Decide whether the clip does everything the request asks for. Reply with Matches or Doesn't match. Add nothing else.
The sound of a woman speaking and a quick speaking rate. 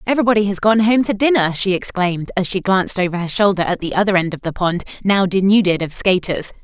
Matches